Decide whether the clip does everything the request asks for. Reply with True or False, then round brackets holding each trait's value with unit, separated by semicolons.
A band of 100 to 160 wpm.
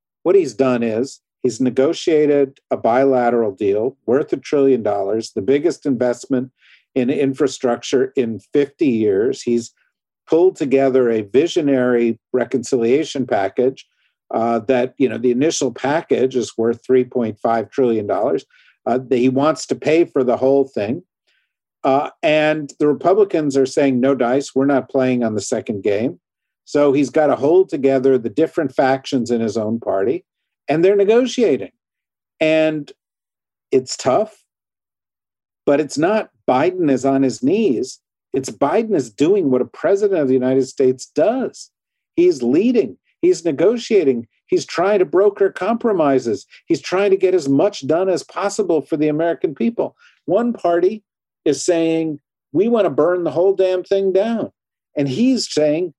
True (155 wpm)